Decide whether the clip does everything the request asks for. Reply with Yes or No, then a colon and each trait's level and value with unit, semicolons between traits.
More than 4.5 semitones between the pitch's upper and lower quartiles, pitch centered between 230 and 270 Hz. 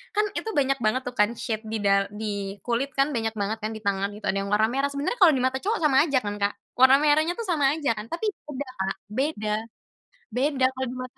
Yes: average, 5.1 semitones; very high, 255 Hz